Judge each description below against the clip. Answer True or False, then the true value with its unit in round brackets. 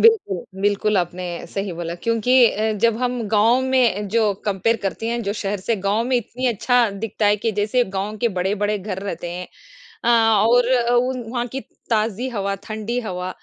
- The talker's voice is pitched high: True (215 Hz)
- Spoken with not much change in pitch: False (3.1 semitones)